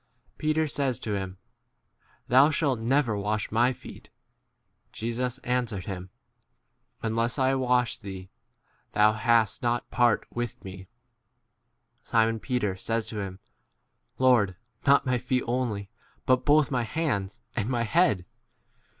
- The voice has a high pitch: No, low, 120 Hz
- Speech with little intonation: No, average, 3.5 semitones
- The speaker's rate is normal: No, slow, 130 wpm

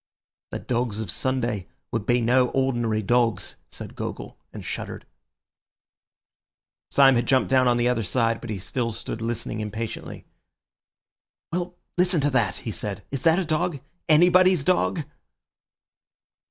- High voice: No, low, 125 Hz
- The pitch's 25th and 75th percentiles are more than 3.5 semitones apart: Yes, average, 4.3 semitones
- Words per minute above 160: No, average, 140 wpm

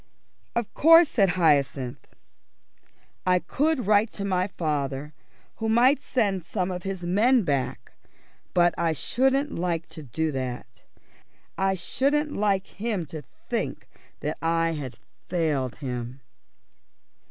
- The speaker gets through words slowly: Yes, slow, 125 wpm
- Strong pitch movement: Yes, wide, 6.3 semitones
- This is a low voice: No, medium, 180 Hz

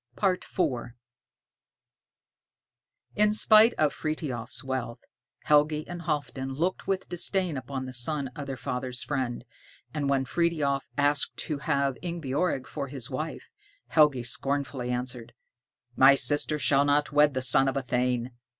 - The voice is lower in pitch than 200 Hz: Yes, medium, 140 Hz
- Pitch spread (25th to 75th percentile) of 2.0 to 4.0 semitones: Yes, average, 3.0 semitones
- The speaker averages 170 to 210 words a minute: No, slow, 135 wpm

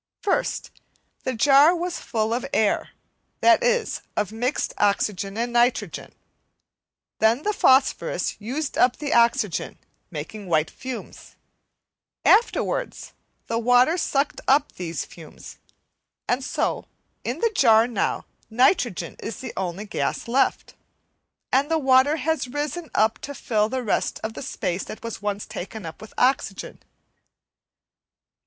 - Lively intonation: No, average, 4.9 semitones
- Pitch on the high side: Yes, high, 240 Hz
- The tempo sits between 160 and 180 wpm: No, slow, 135 wpm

